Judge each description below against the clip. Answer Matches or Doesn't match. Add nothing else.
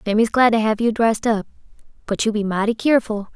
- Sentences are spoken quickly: Matches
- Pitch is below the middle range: Doesn't match